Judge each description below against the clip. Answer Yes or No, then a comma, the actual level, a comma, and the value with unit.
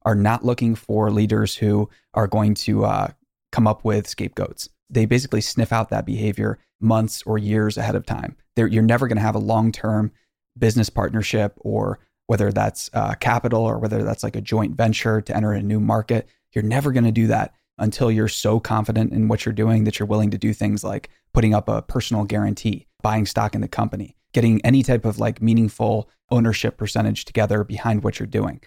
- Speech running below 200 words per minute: No, fast, 205 wpm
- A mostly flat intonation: Yes, narrow, 1.4 semitones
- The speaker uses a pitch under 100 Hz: No, low, 110 Hz